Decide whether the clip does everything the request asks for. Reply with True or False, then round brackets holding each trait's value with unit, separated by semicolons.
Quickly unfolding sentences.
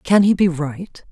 True (215 wpm)